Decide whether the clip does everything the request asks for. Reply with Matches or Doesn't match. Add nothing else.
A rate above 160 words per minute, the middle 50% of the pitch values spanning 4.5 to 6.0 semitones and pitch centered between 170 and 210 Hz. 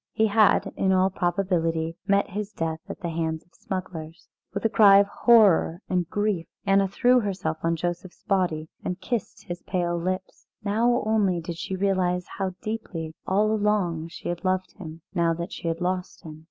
Doesn't match